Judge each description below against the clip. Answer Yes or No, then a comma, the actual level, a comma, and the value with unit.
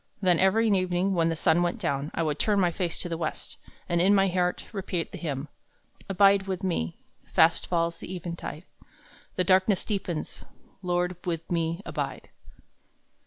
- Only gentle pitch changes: Yes, narrow, 2.3 semitones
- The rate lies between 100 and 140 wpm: No, average, 165 wpm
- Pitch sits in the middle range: Yes, medium, 180 Hz